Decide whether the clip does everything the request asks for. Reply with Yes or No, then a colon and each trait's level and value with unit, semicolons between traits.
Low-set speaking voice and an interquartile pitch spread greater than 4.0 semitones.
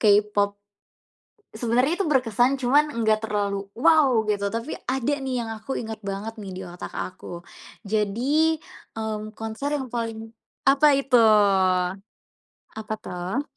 No: high, 225 Hz; average, 4.4 semitones